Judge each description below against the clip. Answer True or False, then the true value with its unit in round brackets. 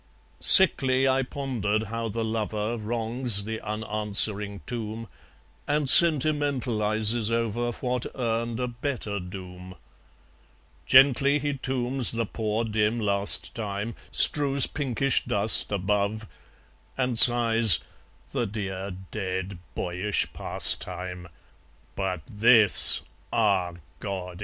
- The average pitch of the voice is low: True (110 Hz)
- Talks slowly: True (100 wpm)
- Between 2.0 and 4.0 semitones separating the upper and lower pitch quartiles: True (3.4 semitones)